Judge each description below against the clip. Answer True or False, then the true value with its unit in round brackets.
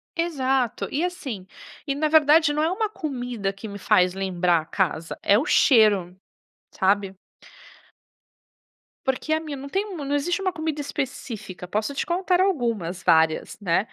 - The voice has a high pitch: True (265 Hz)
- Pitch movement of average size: False (8.4 semitones)